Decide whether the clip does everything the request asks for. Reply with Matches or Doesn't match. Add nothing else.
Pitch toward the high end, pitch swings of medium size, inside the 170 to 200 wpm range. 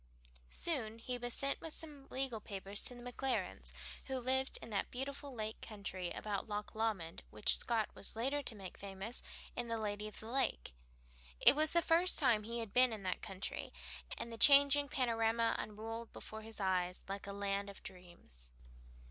Matches